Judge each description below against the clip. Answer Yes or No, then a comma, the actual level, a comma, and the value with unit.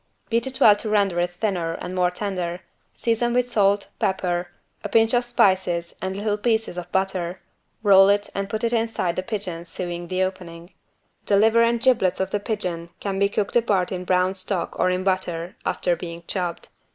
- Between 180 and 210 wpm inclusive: Yes, average, 190 wpm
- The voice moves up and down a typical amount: Yes, average, 3.1 semitones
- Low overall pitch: No, high, 190 Hz